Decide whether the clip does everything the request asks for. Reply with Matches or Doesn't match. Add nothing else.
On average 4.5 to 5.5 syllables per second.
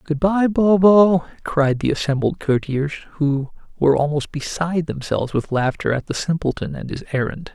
Matches